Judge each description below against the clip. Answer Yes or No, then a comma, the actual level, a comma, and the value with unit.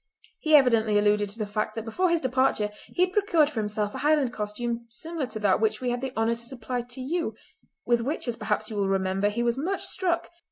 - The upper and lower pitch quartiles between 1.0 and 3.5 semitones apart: No, average, 4.9 semitones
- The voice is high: Yes, high, 235 Hz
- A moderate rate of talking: No, fast, 235 wpm